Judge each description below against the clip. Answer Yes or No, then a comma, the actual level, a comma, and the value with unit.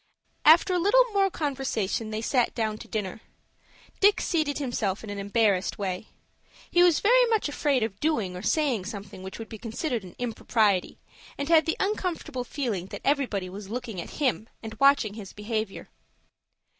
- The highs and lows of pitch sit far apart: Yes, wide, 6.6 semitones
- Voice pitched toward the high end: Yes, high, 230 Hz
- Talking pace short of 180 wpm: Yes, average, 170 wpm